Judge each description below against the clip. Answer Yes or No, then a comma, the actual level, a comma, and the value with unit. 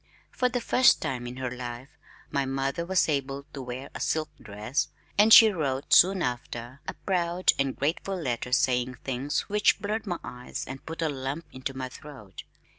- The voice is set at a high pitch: No, low, 135 Hz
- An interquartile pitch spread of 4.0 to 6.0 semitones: Yes, average, 5.0 semitones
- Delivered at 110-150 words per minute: No, average, 185 wpm